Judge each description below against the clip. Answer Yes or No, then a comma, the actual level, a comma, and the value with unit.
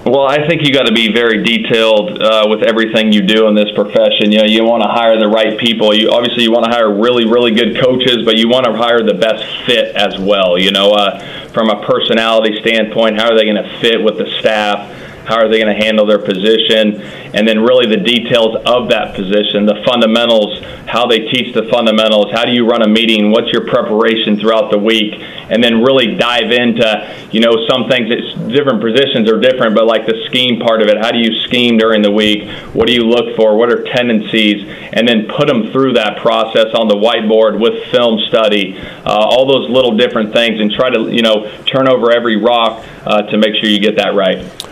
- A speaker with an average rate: No, fast, 225 wpm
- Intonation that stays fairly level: Yes, narrow, 1.7 semitones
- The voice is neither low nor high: No, low, 110 Hz